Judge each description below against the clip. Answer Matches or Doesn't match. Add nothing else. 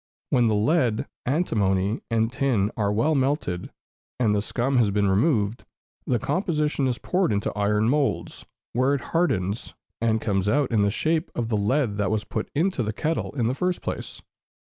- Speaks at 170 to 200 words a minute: Matches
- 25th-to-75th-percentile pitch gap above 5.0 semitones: Matches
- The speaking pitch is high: Doesn't match